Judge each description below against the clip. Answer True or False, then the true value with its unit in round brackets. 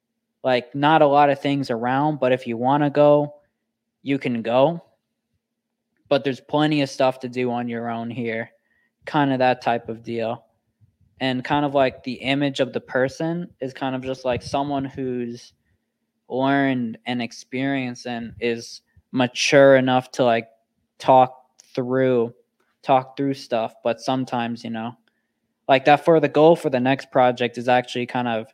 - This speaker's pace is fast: False (170 wpm)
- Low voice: True (130 Hz)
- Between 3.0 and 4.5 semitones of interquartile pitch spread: False (2.6 semitones)